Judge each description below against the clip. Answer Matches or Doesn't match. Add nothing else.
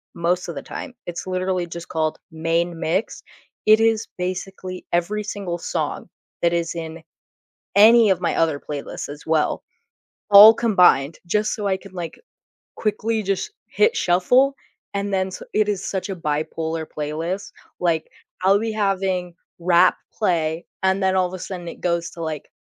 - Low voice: Doesn't match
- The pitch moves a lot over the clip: Doesn't match